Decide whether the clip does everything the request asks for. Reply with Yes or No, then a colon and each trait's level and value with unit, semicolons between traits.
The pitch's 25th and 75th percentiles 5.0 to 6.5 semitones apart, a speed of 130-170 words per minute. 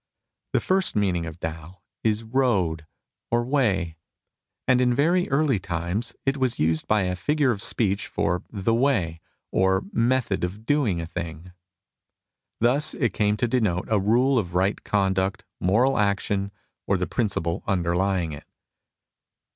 Yes: wide, 5.4 semitones; average, 165 wpm